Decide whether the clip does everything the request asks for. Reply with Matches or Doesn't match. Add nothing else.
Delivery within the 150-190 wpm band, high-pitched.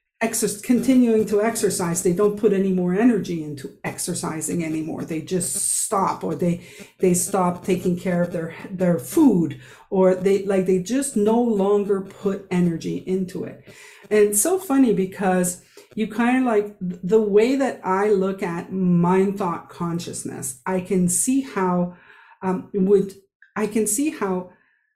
Matches